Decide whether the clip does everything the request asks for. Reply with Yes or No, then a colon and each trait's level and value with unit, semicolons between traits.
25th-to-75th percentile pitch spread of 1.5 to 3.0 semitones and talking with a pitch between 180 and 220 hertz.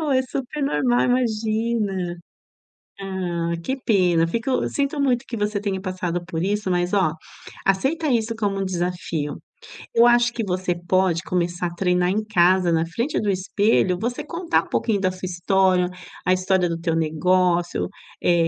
No: average, 4.5 semitones; high, 190 Hz